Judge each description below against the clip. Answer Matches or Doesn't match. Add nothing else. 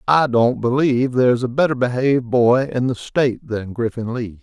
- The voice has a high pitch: Doesn't match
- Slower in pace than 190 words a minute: Doesn't match